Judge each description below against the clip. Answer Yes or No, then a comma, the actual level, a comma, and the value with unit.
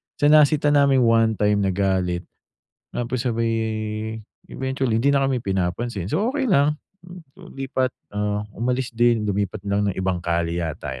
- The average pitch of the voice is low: Yes, low, 115 Hz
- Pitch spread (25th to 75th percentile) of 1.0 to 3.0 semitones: No, wide, 5.7 semitones